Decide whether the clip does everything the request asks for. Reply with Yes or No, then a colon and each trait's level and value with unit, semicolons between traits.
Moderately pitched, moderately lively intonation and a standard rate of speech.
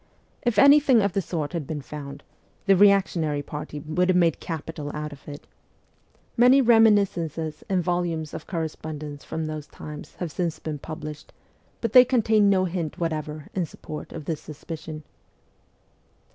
Yes: medium, 165 Hz; average, 4.2 semitones; average, 160 wpm